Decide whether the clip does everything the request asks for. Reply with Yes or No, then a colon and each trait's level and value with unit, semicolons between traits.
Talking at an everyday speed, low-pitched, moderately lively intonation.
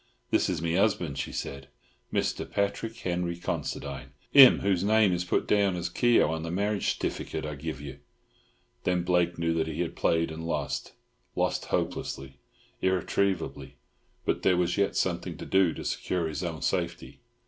Yes: average, 165 wpm; very low, 85 Hz; average, 3.2 semitones